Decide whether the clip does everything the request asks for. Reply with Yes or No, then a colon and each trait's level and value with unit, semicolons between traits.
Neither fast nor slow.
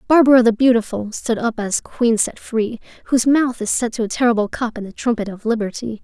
No: fast, 220 wpm